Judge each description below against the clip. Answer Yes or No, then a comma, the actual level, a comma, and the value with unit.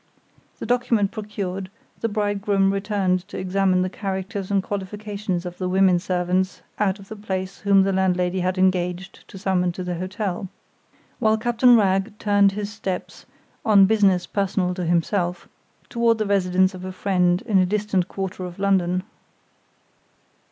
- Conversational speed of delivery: Yes, average, 155 wpm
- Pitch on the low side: No, high, 190 Hz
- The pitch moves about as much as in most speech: No, narrow, 1.9 semitones